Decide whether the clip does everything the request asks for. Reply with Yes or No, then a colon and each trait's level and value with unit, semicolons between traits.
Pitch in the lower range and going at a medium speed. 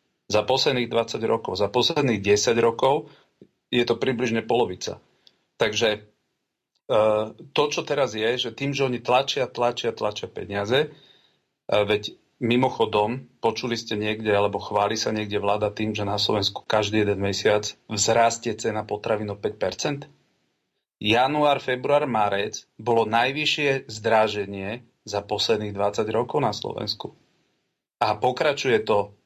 Yes: low, 110 Hz; average, 125 wpm